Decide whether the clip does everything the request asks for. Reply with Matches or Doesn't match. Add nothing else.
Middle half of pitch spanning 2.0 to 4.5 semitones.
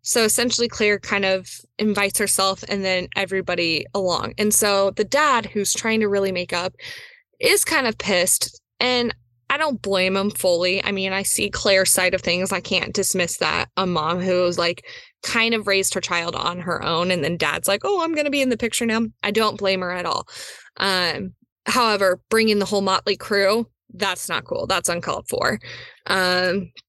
Matches